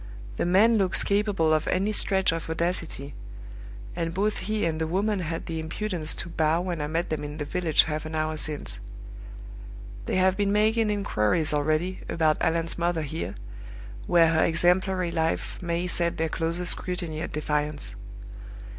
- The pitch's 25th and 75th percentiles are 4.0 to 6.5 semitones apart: No, average, 2.9 semitones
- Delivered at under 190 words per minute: Yes, average, 165 wpm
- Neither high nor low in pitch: Yes, medium, 165 Hz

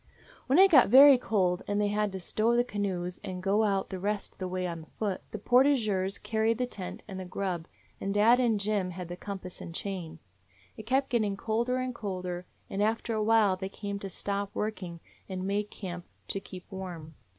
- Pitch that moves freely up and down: No, average, 3.1 semitones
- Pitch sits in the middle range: No, high, 200 Hz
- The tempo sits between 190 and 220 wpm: Yes, average, 200 wpm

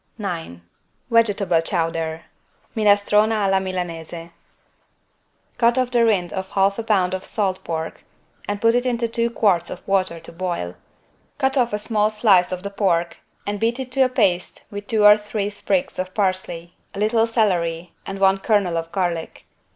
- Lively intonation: No, average, 3.9 semitones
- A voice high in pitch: Yes, high, 195 Hz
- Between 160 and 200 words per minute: Yes, average, 165 wpm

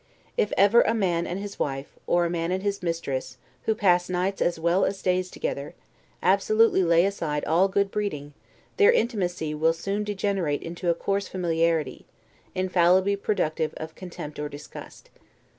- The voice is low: No, medium, 180 Hz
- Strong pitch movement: No, average, 3.3 semitones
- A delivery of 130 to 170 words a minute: Yes, average, 160 wpm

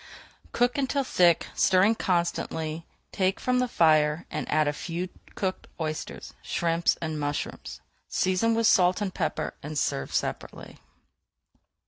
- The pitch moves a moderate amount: Yes, average, 4.2 semitones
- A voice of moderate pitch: Yes, medium, 175 Hz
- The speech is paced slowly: Yes, slow, 130 wpm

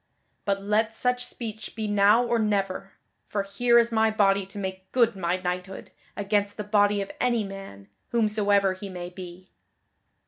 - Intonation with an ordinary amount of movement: No, narrow, 2.3 semitones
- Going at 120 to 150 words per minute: No, average, 165 wpm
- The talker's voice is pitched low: No, high, 205 Hz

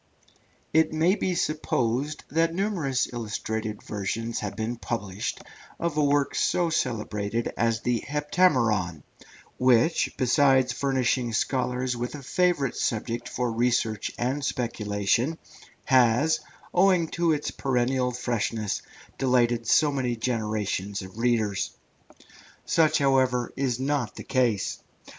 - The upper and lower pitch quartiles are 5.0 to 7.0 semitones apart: No, average, 4.1 semitones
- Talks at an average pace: No, slow, 115 wpm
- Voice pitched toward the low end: Yes, low, 125 Hz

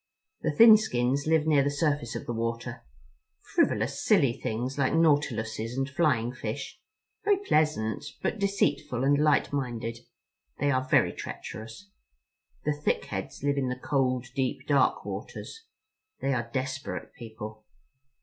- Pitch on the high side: No, low, 135 Hz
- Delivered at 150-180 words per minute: No, average, 140 wpm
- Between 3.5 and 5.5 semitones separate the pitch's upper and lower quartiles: Yes, average, 4.0 semitones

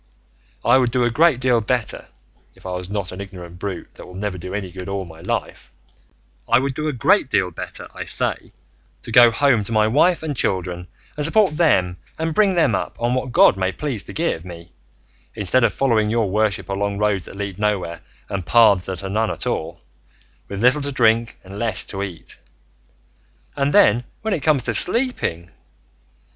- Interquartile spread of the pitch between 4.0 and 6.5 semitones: Yes, wide, 5.6 semitones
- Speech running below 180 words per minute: No, average, 200 wpm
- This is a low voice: Yes, low, 110 Hz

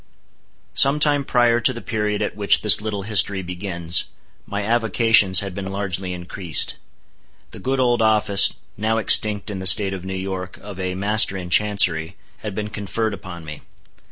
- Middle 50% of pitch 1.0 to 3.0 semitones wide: Yes, average, 2.7 semitones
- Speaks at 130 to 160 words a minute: No, average, 170 wpm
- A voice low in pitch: Yes, low, 100 Hz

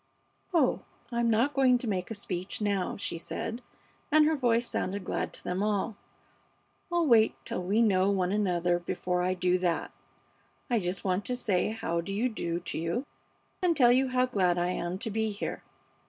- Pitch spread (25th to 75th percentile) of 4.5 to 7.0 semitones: Yes, average, 5.0 semitones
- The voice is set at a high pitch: Yes, high, 205 Hz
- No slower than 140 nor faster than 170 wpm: No, average, 190 wpm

